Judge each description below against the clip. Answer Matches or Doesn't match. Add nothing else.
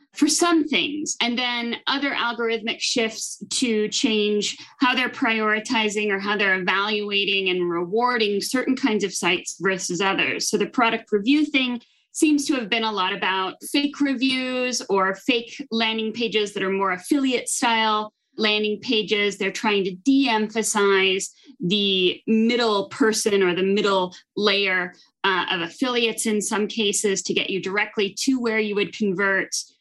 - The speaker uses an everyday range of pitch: Matches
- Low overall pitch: Doesn't match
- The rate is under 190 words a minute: Matches